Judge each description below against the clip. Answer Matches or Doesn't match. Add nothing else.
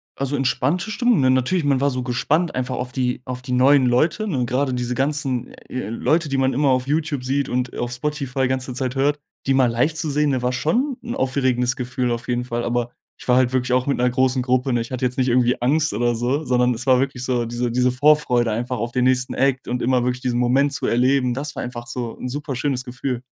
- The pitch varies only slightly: Matches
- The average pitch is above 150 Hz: Doesn't match